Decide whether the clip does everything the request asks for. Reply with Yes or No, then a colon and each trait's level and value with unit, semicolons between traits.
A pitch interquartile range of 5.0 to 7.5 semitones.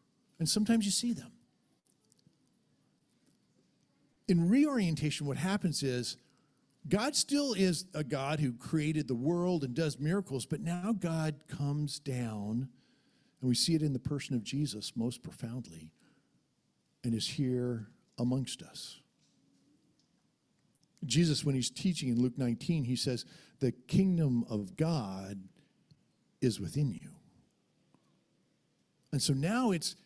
Yes: wide, 5.4 semitones